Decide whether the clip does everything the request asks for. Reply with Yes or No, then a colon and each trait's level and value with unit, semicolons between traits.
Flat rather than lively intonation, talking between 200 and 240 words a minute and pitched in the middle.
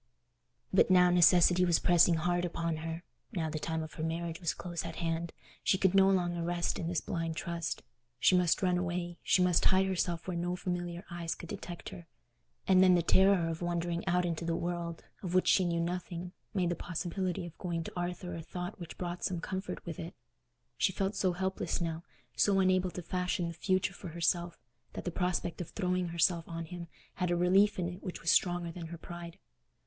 Yes: narrow, 1.3 semitones; fast, 205 wpm; medium, 175 Hz